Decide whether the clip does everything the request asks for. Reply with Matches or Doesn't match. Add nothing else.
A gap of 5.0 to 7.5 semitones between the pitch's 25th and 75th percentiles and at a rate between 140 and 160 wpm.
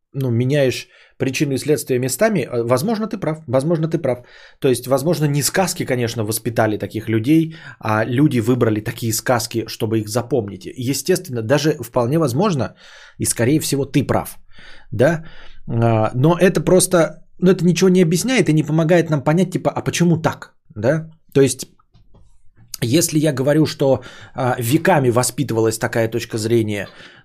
Matches